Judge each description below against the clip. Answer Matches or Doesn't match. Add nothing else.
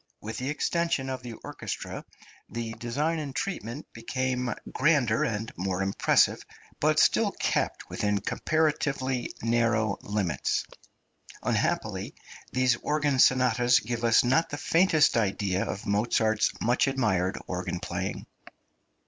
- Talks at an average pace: Doesn't match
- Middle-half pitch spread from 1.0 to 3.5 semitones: Doesn't match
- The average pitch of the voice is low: Matches